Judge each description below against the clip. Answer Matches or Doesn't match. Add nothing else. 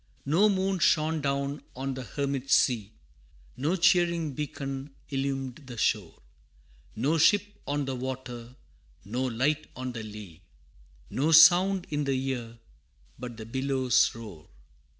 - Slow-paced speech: Matches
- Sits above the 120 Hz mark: Matches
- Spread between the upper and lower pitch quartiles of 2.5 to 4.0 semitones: Matches